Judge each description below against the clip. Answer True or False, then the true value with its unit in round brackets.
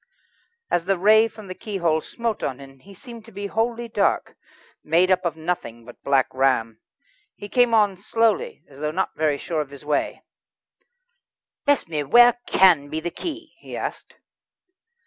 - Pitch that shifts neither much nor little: False (7.3 semitones)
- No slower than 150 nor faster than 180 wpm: True (170 wpm)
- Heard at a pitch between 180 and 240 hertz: True (185 Hz)